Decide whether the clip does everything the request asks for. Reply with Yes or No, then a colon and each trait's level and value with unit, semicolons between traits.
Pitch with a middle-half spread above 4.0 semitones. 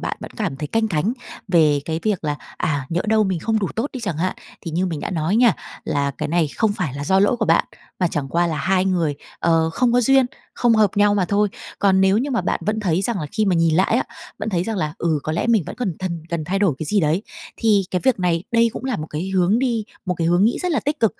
Yes: average, 5.0 semitones